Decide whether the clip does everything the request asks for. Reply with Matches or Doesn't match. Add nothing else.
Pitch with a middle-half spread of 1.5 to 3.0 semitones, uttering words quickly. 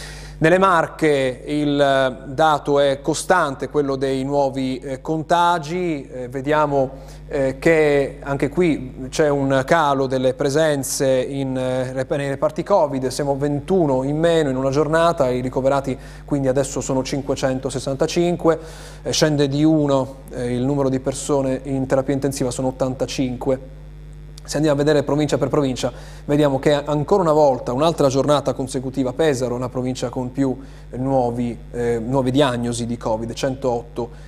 Doesn't match